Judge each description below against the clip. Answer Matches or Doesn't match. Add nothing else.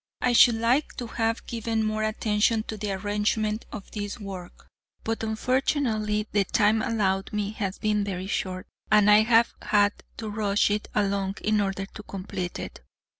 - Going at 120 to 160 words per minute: Doesn't match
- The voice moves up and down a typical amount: Doesn't match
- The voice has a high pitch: Matches